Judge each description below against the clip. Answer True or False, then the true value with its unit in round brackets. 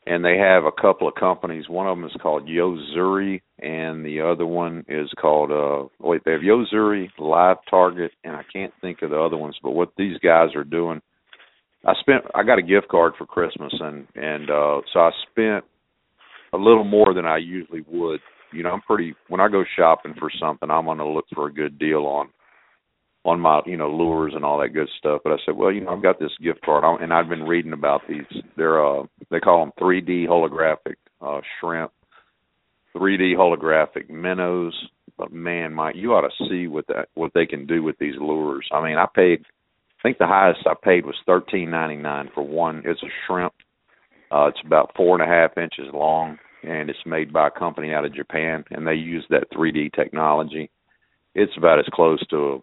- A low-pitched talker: True (80 Hz)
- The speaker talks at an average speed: False (215 wpm)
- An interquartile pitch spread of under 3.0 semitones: True (2.6 semitones)